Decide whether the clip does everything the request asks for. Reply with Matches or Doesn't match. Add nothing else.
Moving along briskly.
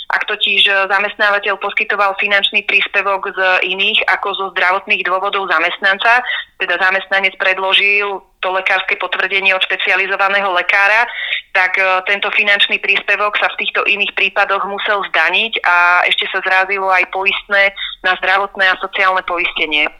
Doesn't match